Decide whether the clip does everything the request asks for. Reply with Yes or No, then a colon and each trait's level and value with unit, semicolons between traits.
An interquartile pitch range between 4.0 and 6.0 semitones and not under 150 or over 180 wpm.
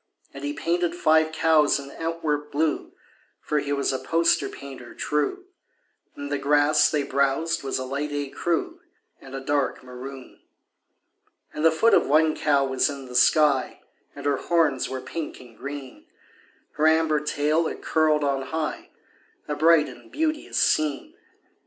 No: narrow, 2.5 semitones; average, 160 wpm